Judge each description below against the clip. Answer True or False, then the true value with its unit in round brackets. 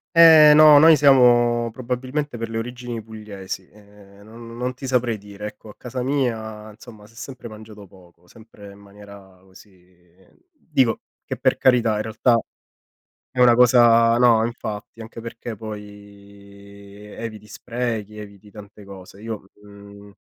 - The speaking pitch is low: True (110 Hz)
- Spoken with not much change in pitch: False (3.1 semitones)